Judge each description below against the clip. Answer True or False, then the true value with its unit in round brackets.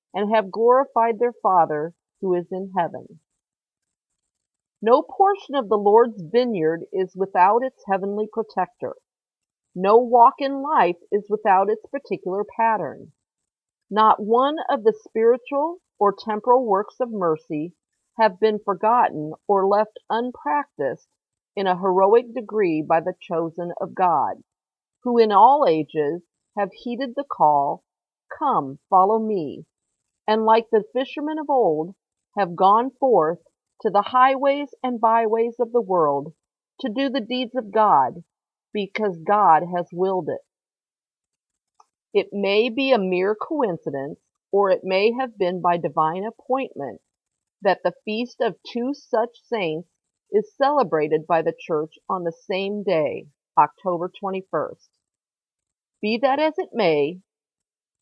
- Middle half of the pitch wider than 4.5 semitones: True (5.2 semitones)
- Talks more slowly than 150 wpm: True (135 wpm)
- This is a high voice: True (215 Hz)